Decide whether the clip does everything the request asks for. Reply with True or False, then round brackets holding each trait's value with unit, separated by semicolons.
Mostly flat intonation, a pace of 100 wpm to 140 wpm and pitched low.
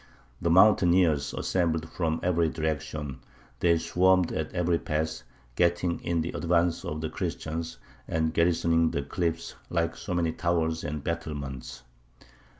True (1.5 semitones; 135 wpm; 85 Hz)